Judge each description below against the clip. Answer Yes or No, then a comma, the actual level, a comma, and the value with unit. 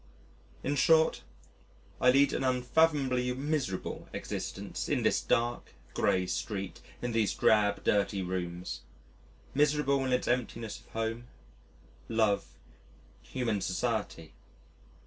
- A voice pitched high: No, low, 120 Hz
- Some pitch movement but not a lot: Yes, average, 4.7 semitones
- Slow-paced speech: Yes, slow, 110 wpm